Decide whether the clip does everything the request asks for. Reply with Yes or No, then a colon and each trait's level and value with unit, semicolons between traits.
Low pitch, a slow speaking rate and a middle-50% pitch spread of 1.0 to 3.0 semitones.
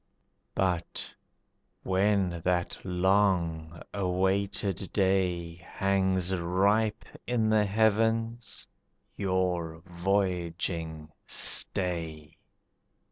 Yes: very low, 95 Hz; slow, 65 wpm; narrow, 2.6 semitones